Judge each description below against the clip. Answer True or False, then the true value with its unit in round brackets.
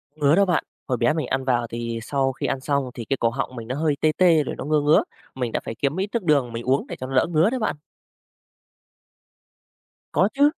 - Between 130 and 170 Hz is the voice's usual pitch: True (140 Hz)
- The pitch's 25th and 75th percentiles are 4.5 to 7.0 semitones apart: False (3.7 semitones)